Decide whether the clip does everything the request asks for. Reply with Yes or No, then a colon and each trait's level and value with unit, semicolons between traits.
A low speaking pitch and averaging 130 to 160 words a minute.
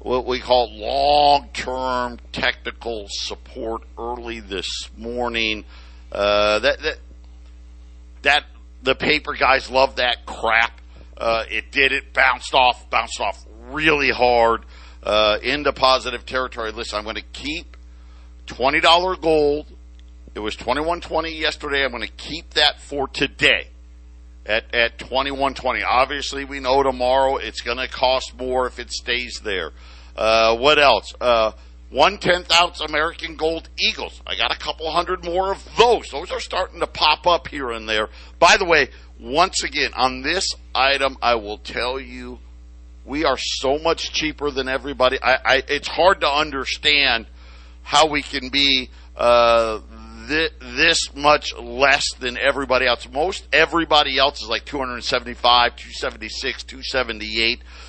Yes: low, 125 Hz; average, 145 wpm